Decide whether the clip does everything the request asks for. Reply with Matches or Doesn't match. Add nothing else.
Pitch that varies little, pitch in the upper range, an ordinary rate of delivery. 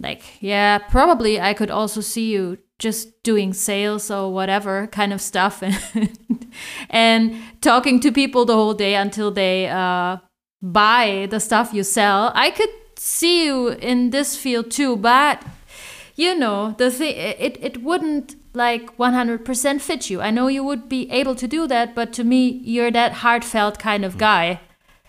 Doesn't match